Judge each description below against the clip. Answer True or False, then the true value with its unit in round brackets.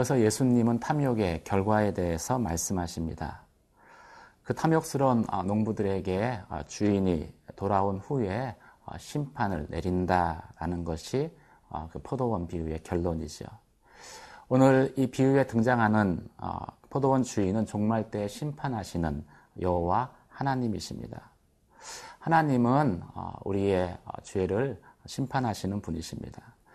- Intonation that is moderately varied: False (6.4 semitones)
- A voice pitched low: True (105 Hz)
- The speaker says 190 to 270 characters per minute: True (260 characters per minute)